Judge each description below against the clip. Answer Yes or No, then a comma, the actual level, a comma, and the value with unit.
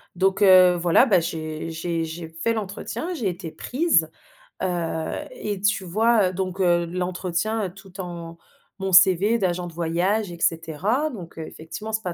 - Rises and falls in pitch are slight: No, average, 3.5 semitones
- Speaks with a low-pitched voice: No, medium, 180 Hz